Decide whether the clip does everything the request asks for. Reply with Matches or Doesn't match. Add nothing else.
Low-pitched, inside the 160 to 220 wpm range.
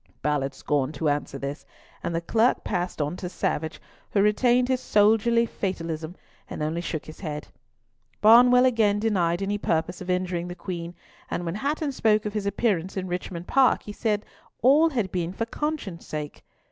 Doesn't match